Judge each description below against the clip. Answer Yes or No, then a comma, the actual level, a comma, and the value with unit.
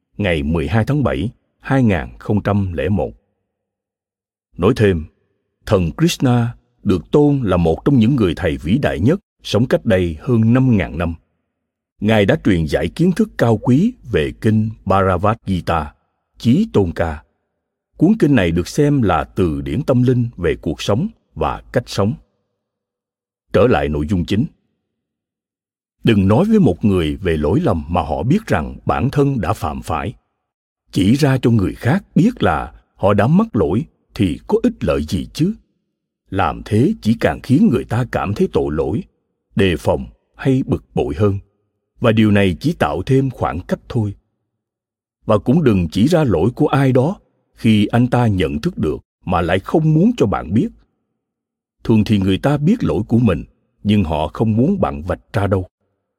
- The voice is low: Yes, low, 110 Hz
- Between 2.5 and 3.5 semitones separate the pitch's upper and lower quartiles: No, wide, 5.4 semitones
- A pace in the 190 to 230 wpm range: No, average, 170 wpm